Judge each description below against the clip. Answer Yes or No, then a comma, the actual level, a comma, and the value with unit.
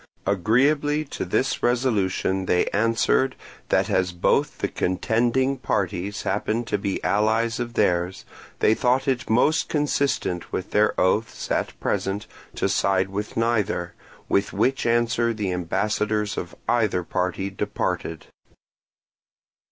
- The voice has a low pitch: Yes, low, 105 Hz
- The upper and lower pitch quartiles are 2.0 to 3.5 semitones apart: No, average, 4.2 semitones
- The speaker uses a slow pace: Yes, slow, 125 wpm